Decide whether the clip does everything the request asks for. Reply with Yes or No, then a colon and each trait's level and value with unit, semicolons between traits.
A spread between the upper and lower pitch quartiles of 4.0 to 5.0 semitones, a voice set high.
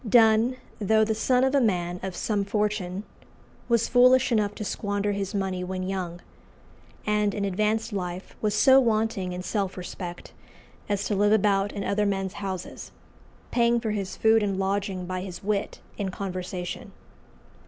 No: narrow, 2.5 semitones; high, 200 Hz